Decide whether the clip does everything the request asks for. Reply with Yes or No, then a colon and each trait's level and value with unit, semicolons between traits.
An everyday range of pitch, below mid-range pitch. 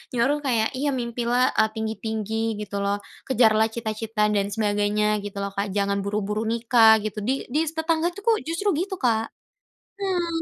No: average, 3.9 semitones; high, 225 Hz